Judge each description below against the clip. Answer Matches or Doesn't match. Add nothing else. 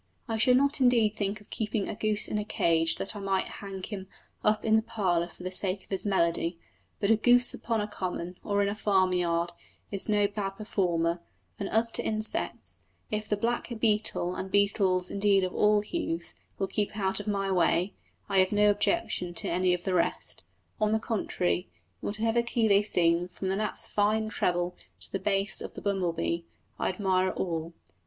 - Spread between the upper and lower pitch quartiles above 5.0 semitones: Doesn't match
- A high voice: Matches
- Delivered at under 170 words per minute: Doesn't match